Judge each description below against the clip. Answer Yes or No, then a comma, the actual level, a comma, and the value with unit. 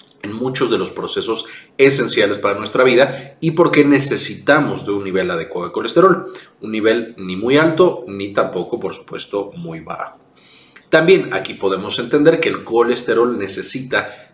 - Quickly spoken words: No, average, 155 wpm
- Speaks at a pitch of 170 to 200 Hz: No, low, 120 Hz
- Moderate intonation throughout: No, wide, 6.1 semitones